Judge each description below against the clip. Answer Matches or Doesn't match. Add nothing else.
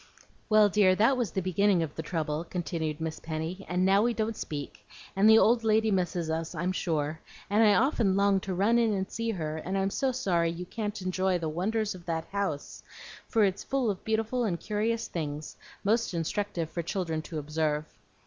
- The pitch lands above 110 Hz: Matches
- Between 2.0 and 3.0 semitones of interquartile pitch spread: Doesn't match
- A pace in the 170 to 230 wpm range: Matches